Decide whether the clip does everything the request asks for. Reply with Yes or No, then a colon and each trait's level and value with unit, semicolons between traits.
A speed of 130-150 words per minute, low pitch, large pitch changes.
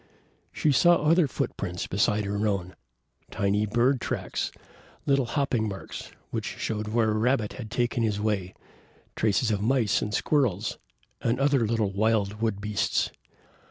No: average, 145 wpm; low, 110 Hz; average, 3.2 semitones